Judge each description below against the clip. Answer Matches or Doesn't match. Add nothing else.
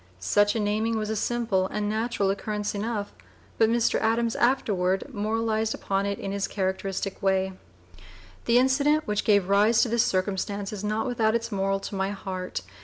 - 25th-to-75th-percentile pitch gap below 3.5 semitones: Matches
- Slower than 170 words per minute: Doesn't match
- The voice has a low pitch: Doesn't match